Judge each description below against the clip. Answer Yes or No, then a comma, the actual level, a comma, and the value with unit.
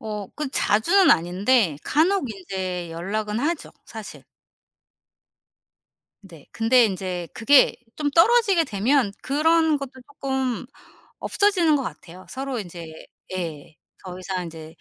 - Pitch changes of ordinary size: No, wide, 8.0 semitones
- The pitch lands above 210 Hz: Yes, high, 220 Hz